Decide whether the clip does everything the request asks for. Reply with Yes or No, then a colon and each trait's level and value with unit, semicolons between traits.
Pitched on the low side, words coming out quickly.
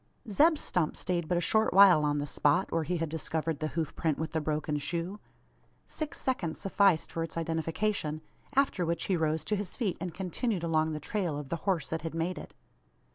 No: medium, 165 Hz; fast, 210 wpm